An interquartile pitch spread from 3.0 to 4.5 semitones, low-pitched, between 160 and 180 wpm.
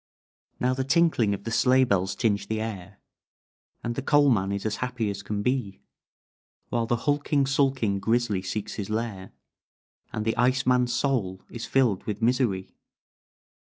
Yes: average, 4.2 semitones; low, 115 Hz; average, 165 wpm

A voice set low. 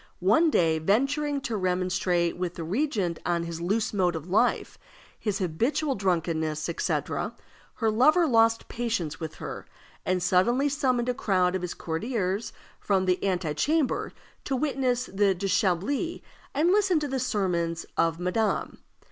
No: high, 195 Hz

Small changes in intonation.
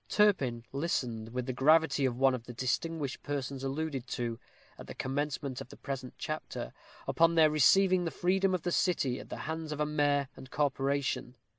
No: average, 3.8 semitones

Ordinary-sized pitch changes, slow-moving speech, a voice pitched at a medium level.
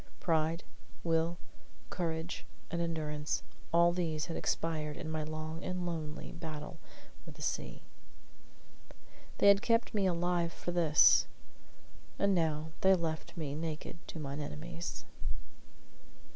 No: narrow, 1.9 semitones; slow, 125 wpm; medium, 165 Hz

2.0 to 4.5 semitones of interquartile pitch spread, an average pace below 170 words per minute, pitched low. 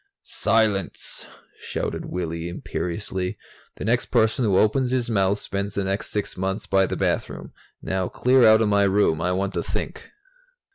Yes: average, 2.7 semitones; average, 160 wpm; low, 100 Hz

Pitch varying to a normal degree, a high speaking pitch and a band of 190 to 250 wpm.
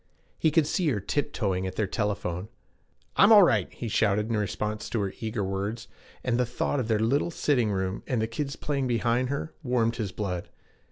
No: average, 4.1 semitones; low, 115 Hz; average, 200 wpm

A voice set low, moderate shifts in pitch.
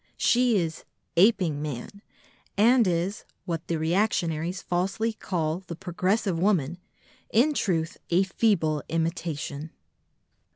No: medium, 175 Hz; average, 3.8 semitones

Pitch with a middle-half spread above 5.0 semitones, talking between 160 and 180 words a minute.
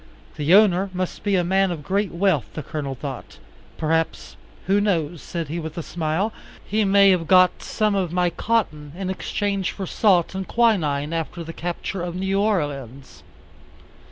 No: average, 3.8 semitones; average, 170 wpm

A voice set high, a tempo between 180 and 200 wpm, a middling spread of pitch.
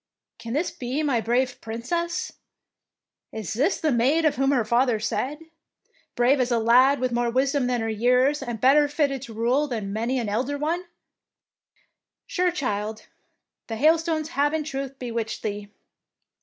No: very high, 255 Hz; average, 170 wpm; average, 3.9 semitones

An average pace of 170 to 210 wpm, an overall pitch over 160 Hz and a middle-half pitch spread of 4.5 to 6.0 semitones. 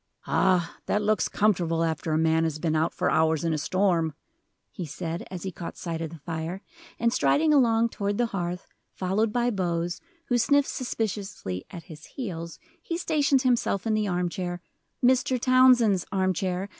Yes: average, 180 wpm; medium, 185 Hz; wide, 5.5 semitones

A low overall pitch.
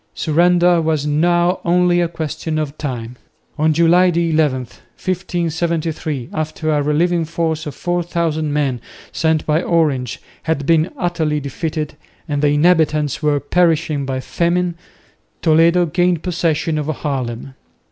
No: medium, 160 Hz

